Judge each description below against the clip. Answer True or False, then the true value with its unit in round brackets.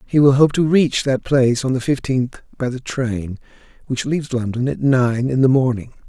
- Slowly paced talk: False (205 wpm)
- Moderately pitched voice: False (130 Hz)